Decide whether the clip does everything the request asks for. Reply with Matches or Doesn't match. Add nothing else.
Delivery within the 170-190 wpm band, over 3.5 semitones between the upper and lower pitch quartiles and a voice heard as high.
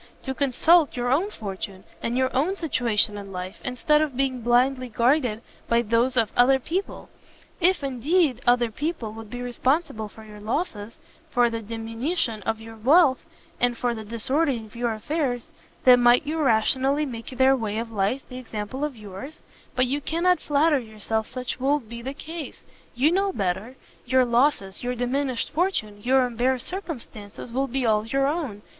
Matches